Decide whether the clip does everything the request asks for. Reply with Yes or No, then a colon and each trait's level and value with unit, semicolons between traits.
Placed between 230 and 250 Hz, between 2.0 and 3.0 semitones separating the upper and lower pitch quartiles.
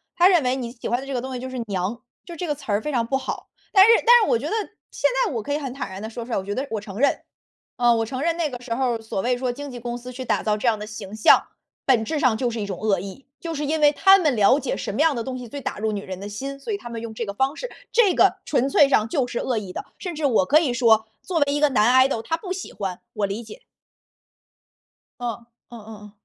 No: high, 245 Hz; average, 4.5 semitones